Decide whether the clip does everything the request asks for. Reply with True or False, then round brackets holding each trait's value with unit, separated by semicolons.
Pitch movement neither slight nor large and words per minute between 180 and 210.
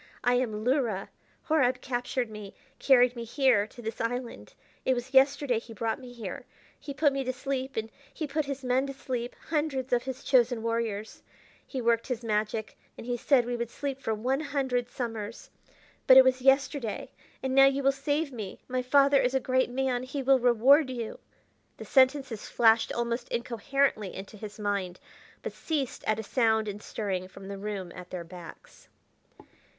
True (3.3 semitones; 185 wpm)